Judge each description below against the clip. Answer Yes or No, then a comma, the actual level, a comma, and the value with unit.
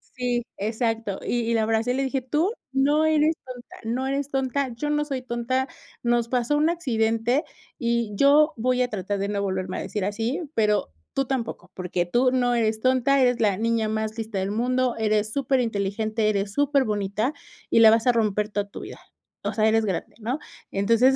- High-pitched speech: Yes, high, 235 Hz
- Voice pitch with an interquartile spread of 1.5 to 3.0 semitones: No, average, 3.4 semitones